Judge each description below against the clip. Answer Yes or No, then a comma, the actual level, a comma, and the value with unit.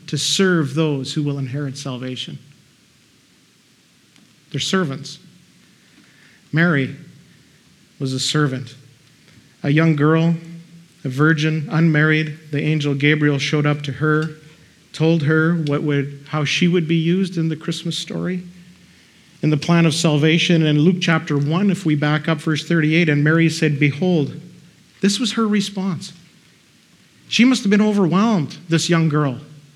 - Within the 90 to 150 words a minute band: Yes, average, 145 wpm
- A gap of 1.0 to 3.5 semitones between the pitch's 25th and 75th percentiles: Yes, narrow, 2.5 semitones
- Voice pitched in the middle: Yes, medium, 155 Hz